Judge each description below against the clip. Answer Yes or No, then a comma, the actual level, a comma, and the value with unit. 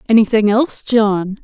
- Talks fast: No, slow, 125 wpm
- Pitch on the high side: Yes, high, 215 Hz